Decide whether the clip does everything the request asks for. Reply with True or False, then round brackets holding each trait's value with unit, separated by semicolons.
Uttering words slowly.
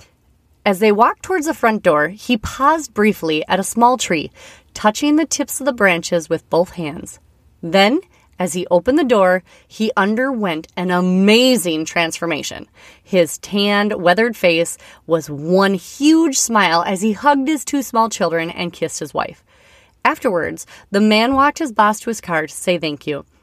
False (170 wpm)